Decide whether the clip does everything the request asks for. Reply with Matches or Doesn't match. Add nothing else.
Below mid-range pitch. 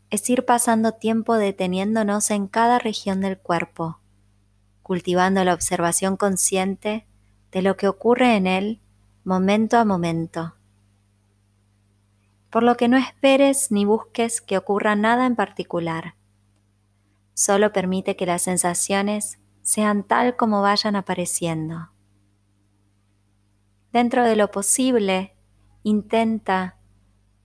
Doesn't match